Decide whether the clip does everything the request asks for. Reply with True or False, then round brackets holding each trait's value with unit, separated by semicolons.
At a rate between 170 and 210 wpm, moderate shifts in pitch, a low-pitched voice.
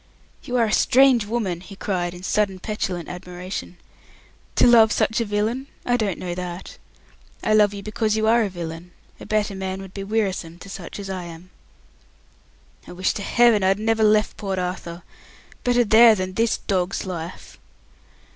False (175 wpm; 3.3 semitones; 195 Hz)